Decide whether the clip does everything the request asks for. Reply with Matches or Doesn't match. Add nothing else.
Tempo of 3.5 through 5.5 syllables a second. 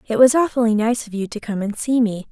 Doesn't match